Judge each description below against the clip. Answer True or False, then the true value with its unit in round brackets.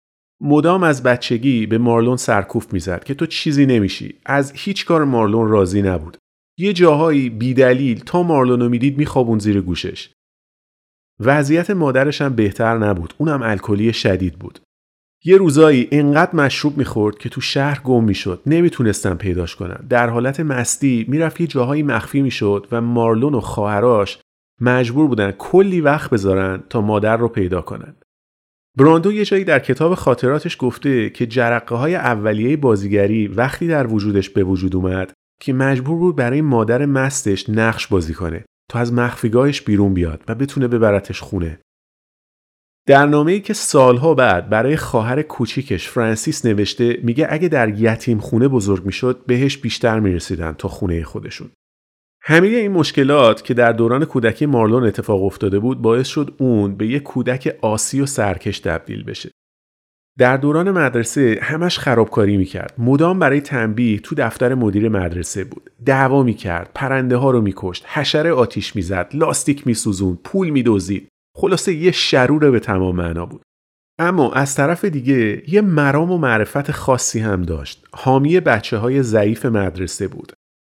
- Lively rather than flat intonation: True (5.7 semitones)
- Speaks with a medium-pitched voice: False (120 Hz)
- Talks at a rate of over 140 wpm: True (150 wpm)